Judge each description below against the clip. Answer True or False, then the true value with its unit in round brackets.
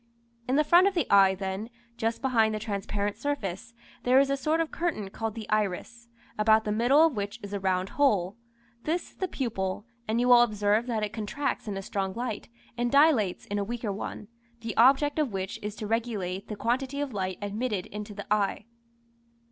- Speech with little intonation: False (4.0 semitones)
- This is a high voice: True (220 Hz)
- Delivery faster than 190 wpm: True (205 wpm)